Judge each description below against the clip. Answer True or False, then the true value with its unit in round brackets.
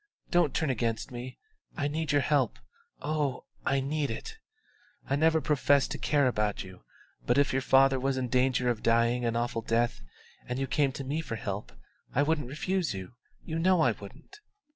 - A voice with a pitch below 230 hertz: True (135 Hz)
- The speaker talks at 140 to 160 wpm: False (185 wpm)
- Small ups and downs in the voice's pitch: False (3.8 semitones)